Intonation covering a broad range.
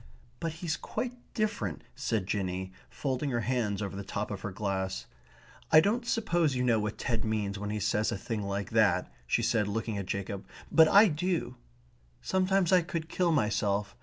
Yes: wide, 8.3 semitones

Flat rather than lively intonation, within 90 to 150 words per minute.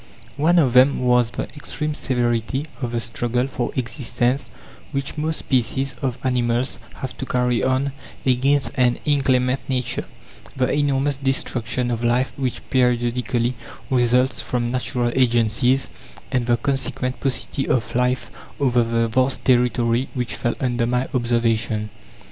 Yes: narrow, 1.9 semitones; slow, 135 wpm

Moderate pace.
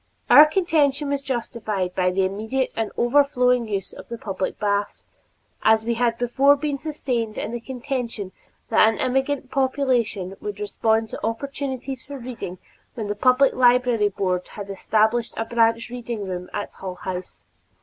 Yes: average, 160 wpm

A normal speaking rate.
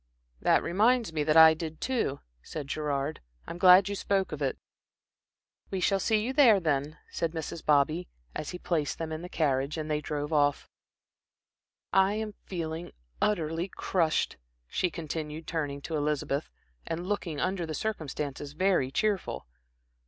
Yes: average, 155 wpm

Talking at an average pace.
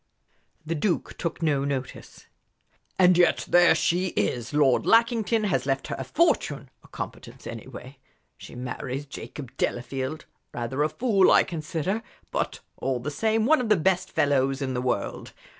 Yes: average, 160 wpm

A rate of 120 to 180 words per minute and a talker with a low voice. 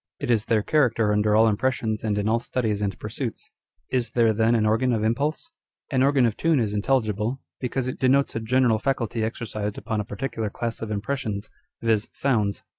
No: average, 190 wpm; low, 115 Hz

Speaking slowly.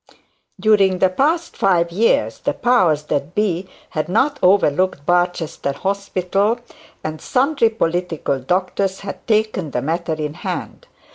Yes: slow, 130 wpm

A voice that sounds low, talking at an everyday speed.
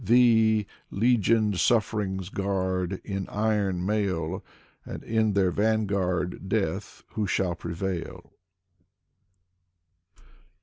No: low, 100 Hz; slow, 85 wpm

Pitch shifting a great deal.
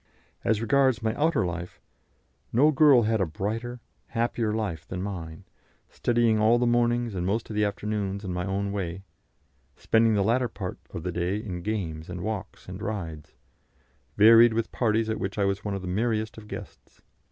No: average, 3.4 semitones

